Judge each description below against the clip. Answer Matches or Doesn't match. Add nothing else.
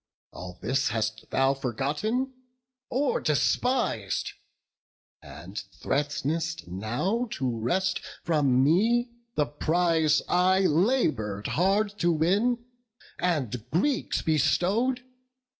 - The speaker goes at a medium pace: Doesn't match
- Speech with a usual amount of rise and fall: Doesn't match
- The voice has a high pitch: Doesn't match